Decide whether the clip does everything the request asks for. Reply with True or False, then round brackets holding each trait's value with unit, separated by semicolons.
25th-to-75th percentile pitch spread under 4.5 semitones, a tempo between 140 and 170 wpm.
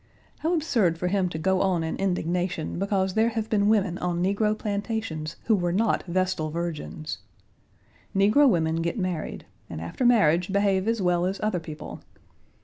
True (3.6 semitones; 165 wpm)